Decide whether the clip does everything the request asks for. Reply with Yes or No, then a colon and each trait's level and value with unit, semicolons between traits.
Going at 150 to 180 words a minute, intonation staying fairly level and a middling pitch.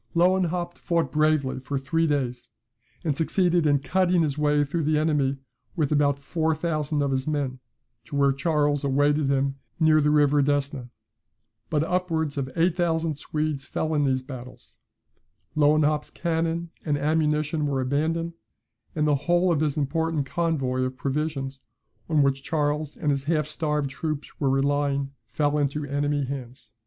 Yes: average, 160 wpm; narrow, 2.3 semitones; medium, 150 Hz